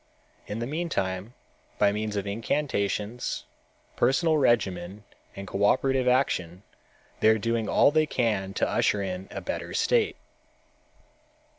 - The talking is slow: Yes, slow, 125 wpm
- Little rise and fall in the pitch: No, average, 4.8 semitones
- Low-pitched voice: Yes, low, 110 Hz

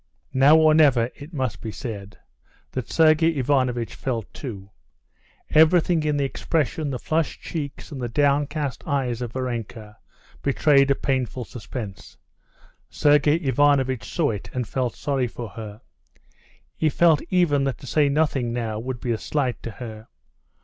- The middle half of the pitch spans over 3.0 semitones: Yes, average, 3.9 semitones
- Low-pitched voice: Yes, low, 130 Hz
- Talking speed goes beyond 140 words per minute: Yes, average, 150 wpm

